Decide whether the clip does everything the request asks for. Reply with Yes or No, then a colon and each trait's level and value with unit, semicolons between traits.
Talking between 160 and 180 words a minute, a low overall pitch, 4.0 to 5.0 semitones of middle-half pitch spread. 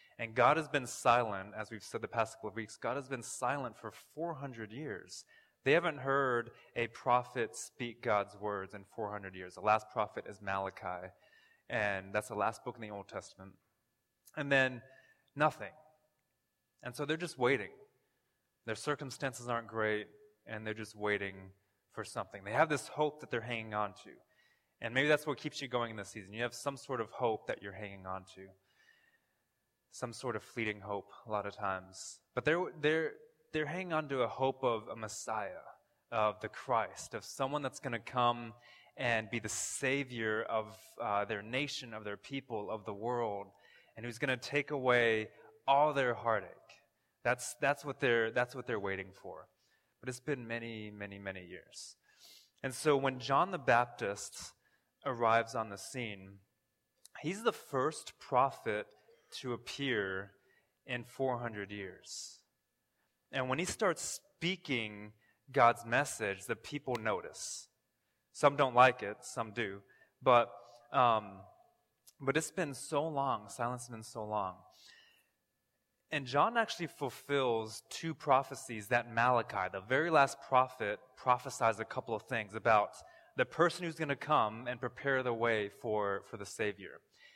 Yes: average, 165 wpm; low, 120 Hz; average, 4.4 semitones